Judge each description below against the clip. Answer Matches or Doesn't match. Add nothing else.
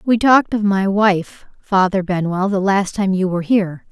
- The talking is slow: Doesn't match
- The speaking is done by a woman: Matches